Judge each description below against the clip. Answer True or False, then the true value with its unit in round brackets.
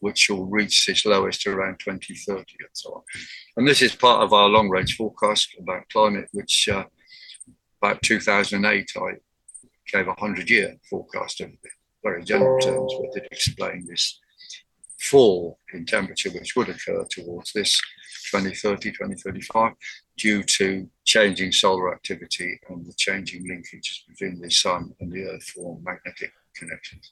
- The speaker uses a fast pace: False (140 wpm)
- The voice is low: True (130 Hz)